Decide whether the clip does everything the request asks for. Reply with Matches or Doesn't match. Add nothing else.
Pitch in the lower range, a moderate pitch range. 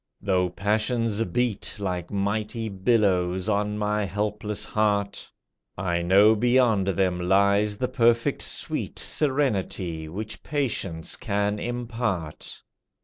Matches